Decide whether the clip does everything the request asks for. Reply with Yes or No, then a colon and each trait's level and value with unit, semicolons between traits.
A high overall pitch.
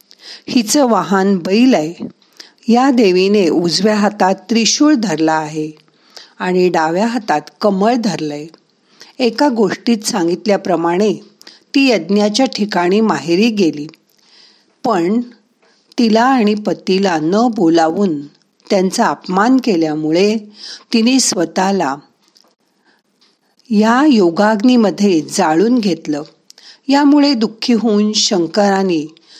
Yes: high, 205 Hz